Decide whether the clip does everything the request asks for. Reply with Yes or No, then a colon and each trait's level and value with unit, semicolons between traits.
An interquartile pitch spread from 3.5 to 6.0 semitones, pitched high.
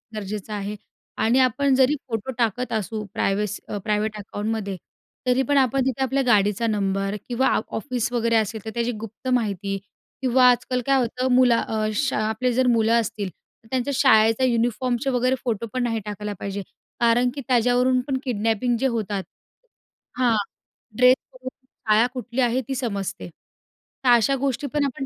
No: average, 3.0 semitones; high, 235 Hz